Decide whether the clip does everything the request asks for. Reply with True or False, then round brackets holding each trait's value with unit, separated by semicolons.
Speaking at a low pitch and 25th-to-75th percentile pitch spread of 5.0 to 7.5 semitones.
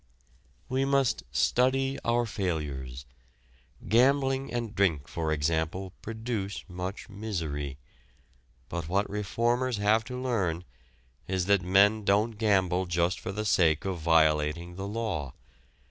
True (100 Hz; 5.4 semitones)